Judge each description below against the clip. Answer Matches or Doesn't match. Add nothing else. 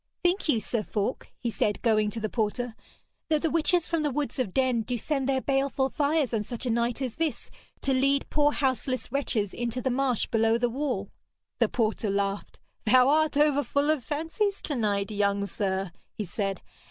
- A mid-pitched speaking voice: Doesn't match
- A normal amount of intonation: Matches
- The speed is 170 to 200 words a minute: Matches